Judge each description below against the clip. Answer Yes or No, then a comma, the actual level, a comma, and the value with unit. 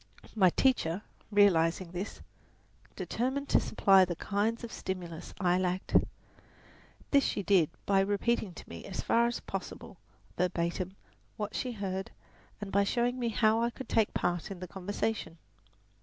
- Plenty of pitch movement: No, average, 3.7 semitones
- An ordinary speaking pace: Yes, average, 150 wpm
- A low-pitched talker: No, high, 200 Hz